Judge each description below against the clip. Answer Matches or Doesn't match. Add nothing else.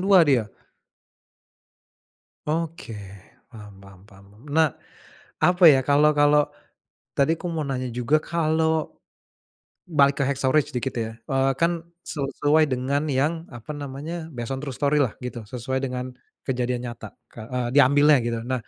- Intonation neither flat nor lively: Matches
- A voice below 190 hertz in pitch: Matches